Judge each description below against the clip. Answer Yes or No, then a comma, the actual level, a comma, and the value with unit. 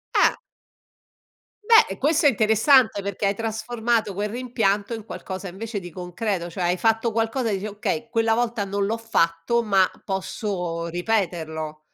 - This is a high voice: Yes, high, 210 Hz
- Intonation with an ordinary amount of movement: Yes, average, 3.5 semitones